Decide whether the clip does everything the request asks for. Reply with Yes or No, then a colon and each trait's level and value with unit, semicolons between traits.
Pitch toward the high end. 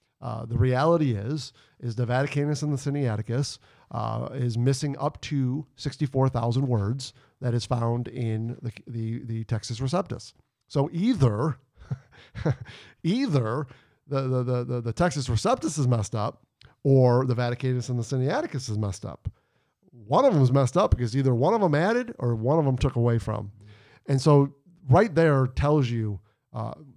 No: low, 130 Hz